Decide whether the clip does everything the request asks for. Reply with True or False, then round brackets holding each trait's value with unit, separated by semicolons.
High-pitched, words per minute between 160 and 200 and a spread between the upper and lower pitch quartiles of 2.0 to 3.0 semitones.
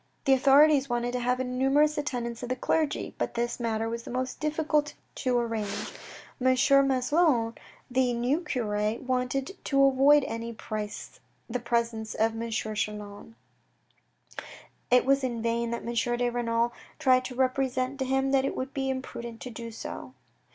True (250 Hz; 165 wpm; 2.5 semitones)